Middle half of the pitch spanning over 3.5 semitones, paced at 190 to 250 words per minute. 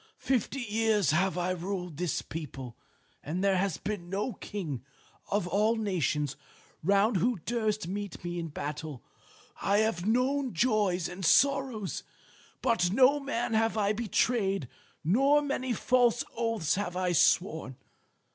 No: average, 4.8 semitones; average, 140 wpm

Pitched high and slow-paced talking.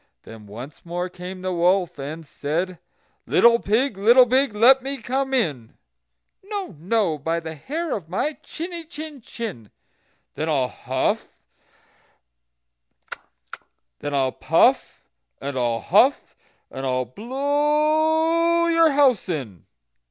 Yes: high, 200 Hz; slow, 115 wpm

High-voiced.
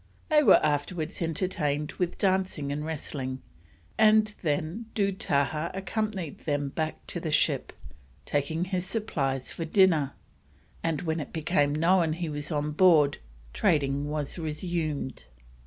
No: medium, 160 Hz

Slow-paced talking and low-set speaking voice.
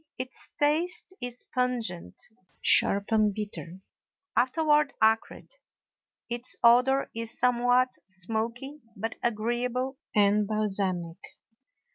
No: slow, 90 wpm; high, 235 Hz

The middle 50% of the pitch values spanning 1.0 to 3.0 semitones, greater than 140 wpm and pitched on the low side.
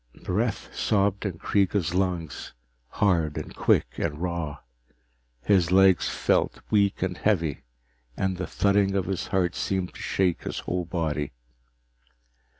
No: narrow, 2.6 semitones; slow, 135 wpm; very low, 90 Hz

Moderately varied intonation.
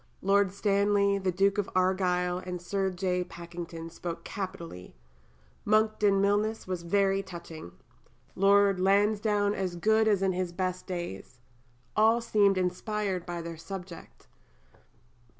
No: narrow, 2.3 semitones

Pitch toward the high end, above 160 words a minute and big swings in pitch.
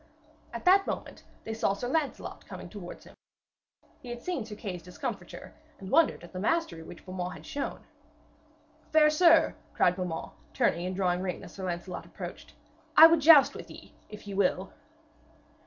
Yes: high, 200 Hz; average, 170 wpm; wide, 9.0 semitones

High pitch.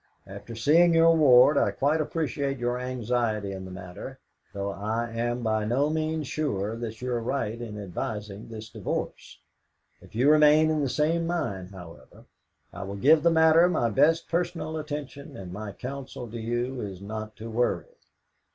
No: low, 120 Hz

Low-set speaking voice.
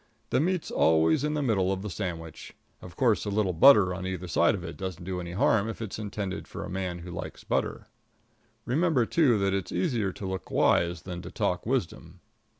Yes: very low, 95 Hz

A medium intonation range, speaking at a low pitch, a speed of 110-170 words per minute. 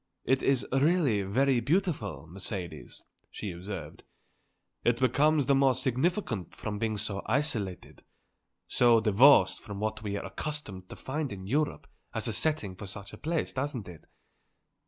No: wide, 5.7 semitones; low, 115 Hz; average, 150 wpm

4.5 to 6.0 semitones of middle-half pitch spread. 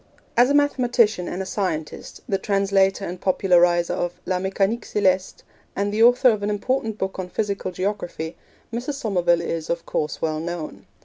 No: average, 3.4 semitones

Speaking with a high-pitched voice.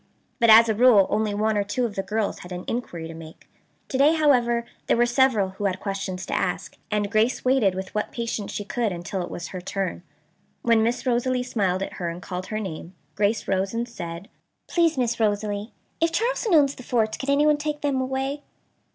Yes: high, 220 Hz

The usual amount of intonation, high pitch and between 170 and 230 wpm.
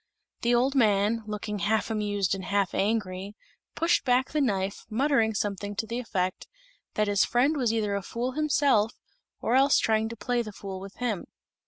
Yes: average, 3.4 semitones; high, 220 Hz; average, 180 wpm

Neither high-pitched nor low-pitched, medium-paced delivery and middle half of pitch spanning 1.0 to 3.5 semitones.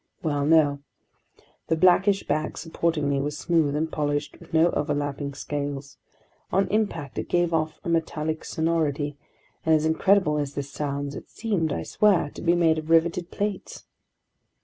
Yes: medium, 155 Hz; average, 160 wpm; average, 2.7 semitones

